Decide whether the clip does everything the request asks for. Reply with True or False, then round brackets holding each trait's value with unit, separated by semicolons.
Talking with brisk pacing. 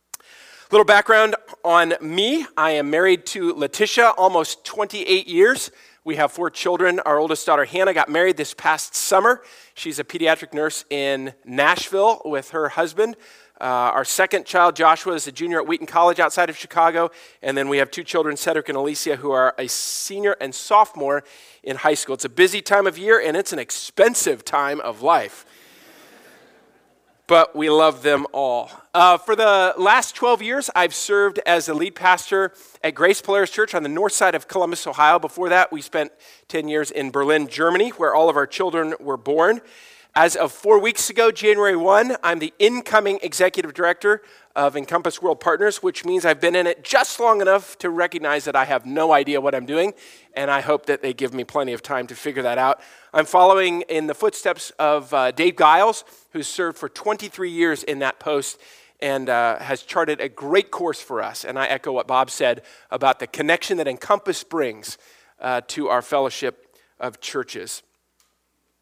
False (190 wpm)